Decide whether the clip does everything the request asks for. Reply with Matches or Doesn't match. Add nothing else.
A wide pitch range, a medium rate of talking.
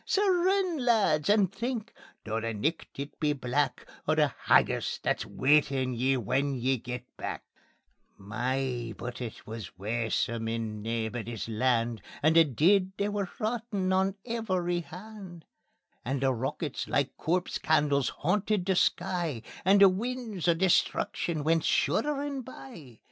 Matches